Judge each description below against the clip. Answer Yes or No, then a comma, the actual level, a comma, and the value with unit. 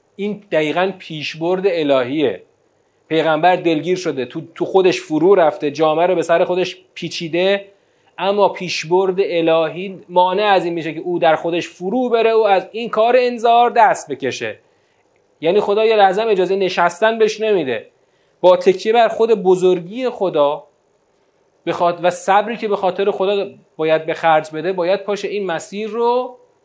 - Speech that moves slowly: No, average, 150 wpm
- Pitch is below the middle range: No, high, 190 Hz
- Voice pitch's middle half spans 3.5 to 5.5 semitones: Yes, average, 4.2 semitones